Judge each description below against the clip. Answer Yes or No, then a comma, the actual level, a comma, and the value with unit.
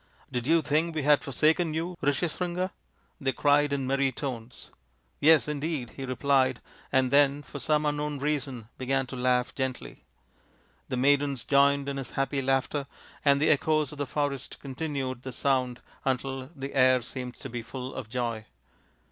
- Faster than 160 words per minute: Yes, average, 180 wpm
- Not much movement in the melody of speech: Yes, narrow, 2.3 semitones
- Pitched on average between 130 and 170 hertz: Yes, low, 135 Hz